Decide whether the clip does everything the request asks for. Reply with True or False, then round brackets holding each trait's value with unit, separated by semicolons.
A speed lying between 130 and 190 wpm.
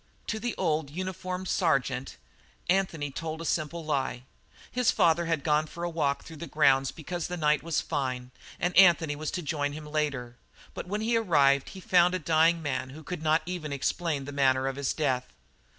False (200 wpm)